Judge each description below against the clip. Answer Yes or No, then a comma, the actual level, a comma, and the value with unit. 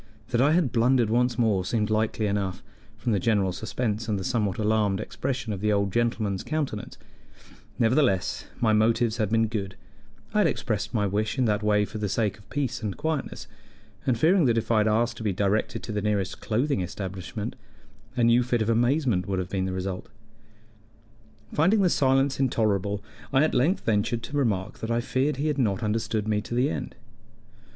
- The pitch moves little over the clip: No, average, 3.3 semitones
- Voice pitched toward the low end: Yes, low, 110 Hz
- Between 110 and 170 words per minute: No, average, 195 wpm